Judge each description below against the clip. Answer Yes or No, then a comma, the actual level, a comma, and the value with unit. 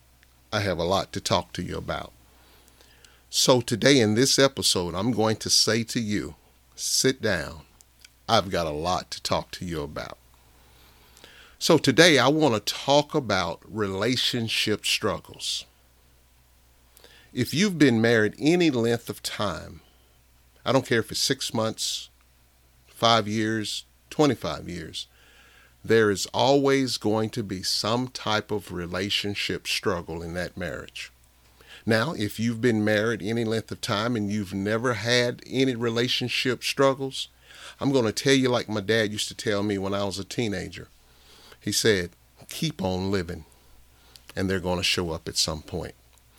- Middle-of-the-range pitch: No, low, 100 Hz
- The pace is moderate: Yes, average, 155 wpm